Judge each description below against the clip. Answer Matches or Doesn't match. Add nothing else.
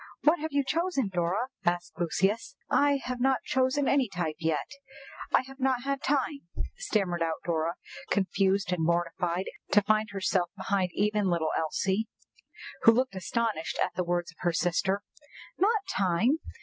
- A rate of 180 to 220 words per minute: Doesn't match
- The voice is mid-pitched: Doesn't match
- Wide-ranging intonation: Matches